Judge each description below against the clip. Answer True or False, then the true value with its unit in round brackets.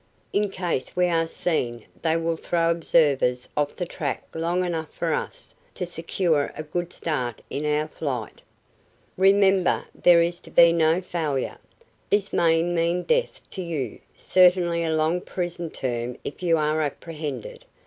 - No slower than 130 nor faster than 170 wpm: True (155 wpm)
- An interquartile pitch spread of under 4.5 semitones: True (2.6 semitones)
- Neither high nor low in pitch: True (165 Hz)